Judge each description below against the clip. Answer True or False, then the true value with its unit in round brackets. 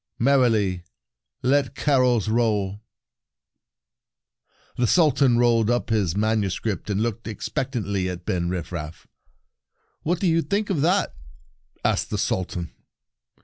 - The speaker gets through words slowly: True (120 wpm)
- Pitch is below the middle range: True (115 Hz)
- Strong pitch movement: True (5.7 semitones)